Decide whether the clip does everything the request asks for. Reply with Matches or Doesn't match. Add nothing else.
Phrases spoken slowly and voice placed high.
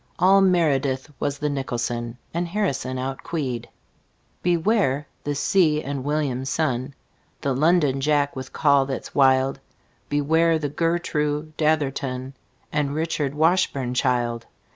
Doesn't match